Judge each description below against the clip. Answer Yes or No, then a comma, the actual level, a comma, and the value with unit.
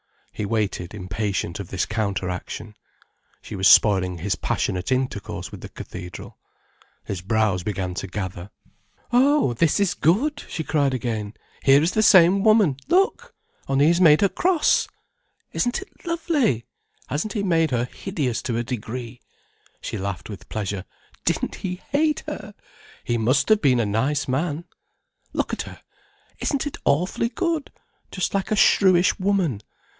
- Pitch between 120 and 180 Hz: Yes, low, 135 Hz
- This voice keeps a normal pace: Yes, average, 145 wpm